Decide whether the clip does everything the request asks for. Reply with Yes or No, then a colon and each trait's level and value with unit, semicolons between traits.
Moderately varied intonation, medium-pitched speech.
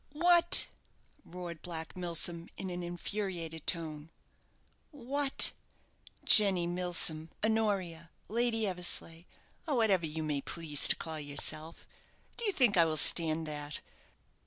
Yes: average, 4.6 semitones; medium, 175 Hz